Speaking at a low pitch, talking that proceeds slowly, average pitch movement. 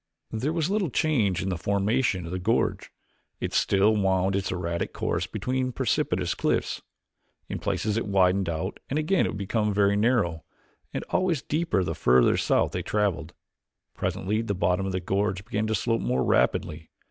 No: low, 100 Hz; average, 170 wpm; average, 4.0 semitones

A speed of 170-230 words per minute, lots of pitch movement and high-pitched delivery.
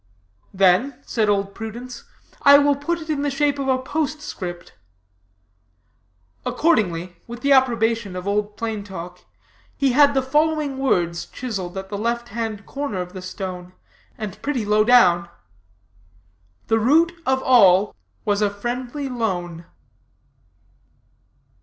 No: slow, 135 wpm; wide, 5.9 semitones; high, 230 Hz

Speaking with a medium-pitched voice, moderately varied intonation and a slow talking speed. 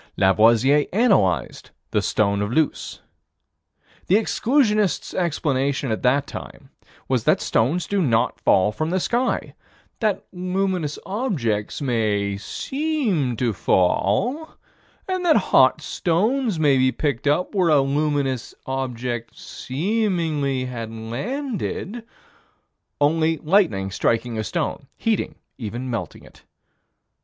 No: medium, 145 Hz; wide, 8.6 semitones; slow, 115 wpm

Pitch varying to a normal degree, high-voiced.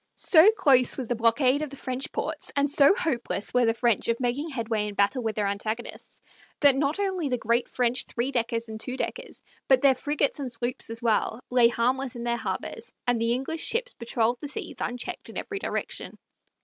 Yes: average, 3.3 semitones; very high, 250 Hz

